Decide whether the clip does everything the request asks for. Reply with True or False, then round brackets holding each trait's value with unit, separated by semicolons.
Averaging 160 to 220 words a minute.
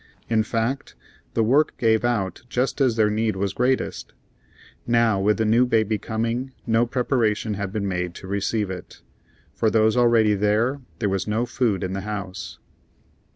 True (165 wpm)